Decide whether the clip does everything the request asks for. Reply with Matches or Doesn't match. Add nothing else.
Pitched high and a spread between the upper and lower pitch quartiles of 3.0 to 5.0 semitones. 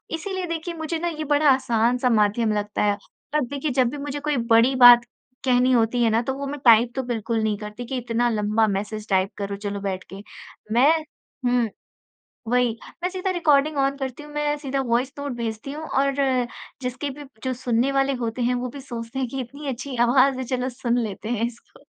Matches